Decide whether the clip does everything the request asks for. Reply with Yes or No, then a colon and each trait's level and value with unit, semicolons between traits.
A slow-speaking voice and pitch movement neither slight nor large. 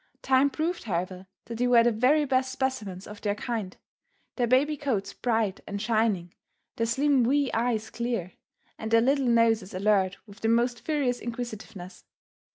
No: average, 165 wpm; average, 3.8 semitones